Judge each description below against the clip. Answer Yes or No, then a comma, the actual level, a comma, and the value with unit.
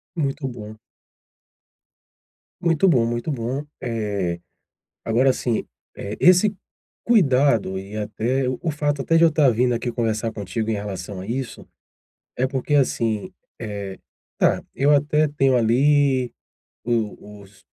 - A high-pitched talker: No, low, 125 Hz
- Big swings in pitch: No, average, 4.8 semitones